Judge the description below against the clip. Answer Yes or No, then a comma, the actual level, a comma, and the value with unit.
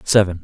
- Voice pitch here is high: No, very low, 95 Hz